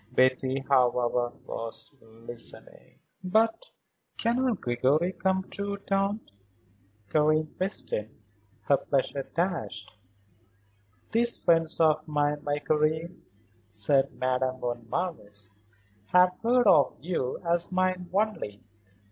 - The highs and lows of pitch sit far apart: Yes, wide, 6.5 semitones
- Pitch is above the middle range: No, medium, 155 Hz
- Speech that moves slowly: Yes, slow, 100 wpm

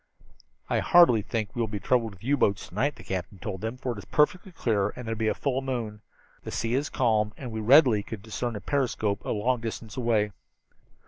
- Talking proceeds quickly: Yes, fast, 235 wpm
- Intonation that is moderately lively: Yes, average, 3.3 semitones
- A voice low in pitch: Yes, low, 115 Hz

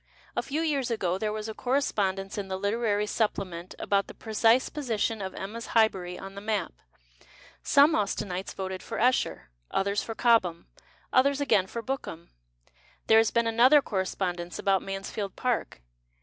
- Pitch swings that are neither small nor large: Yes, average, 3.4 semitones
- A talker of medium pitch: No, high, 210 Hz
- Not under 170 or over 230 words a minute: No, average, 160 wpm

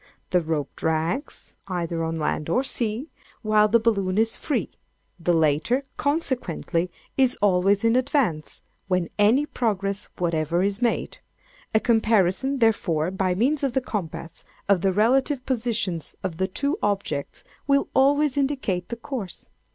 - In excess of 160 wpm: No, average, 145 wpm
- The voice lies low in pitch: No, high, 205 Hz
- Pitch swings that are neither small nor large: No, wide, 6.4 semitones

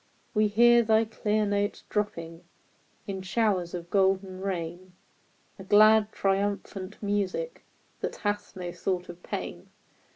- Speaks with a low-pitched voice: No, high, 200 Hz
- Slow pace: Yes, slow, 125 wpm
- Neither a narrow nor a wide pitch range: No, narrow, 2.3 semitones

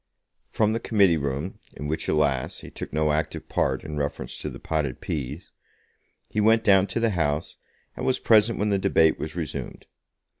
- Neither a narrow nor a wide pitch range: No, wide, 5.9 semitones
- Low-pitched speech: Yes, very low, 80 Hz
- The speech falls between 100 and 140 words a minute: No, average, 185 wpm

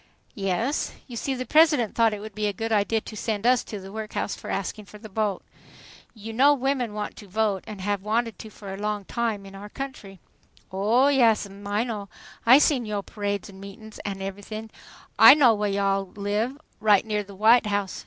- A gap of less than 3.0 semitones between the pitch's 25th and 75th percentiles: Yes, narrow, 2.4 semitones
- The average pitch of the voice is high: Yes, high, 210 Hz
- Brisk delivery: Yes, fast, 210 wpm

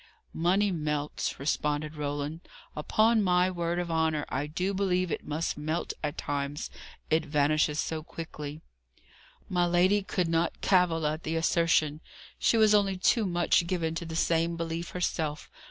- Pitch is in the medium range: Yes, medium, 165 Hz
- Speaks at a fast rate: No, average, 155 wpm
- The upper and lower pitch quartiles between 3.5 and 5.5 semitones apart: No, average, 2.9 semitones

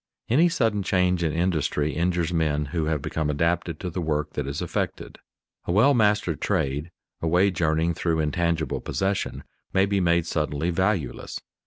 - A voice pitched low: Yes, very low, 85 Hz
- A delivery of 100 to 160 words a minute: No, average, 170 wpm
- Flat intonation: No, average, 3.2 semitones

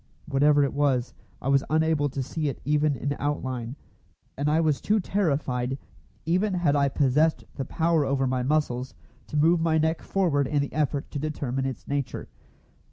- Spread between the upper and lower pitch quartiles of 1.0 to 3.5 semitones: Yes, average, 2.8 semitones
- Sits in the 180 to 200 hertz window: No, medium, 145 Hz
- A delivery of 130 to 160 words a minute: No, average, 175 wpm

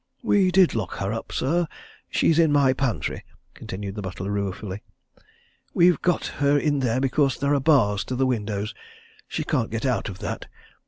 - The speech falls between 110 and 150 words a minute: No, average, 175 wpm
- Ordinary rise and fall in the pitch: No, wide, 5.9 semitones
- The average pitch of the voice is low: Yes, low, 130 Hz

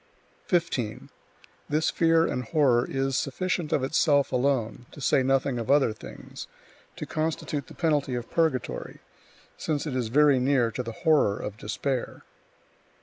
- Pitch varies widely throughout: No, average, 3.7 semitones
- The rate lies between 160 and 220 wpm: No, average, 145 wpm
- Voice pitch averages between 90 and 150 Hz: Yes, low, 135 Hz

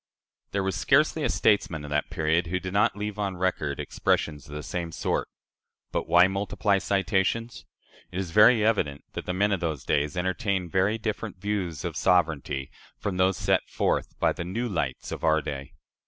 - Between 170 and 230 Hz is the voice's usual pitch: No, very low, 95 Hz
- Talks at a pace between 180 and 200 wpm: Yes, average, 185 wpm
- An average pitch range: Yes, average, 4.2 semitones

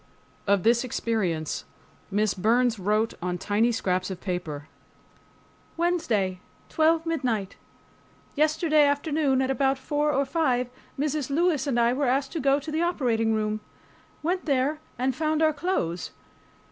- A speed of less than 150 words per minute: Yes, average, 140 wpm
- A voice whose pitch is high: Yes, very high, 260 Hz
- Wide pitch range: Yes, wide, 6.1 semitones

